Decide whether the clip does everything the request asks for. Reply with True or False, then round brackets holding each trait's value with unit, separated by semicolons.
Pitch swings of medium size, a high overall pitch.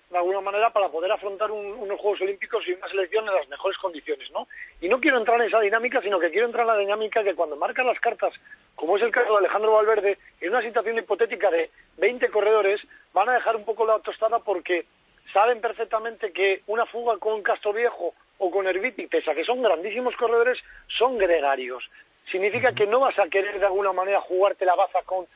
True (3.0 semitones; 215 Hz)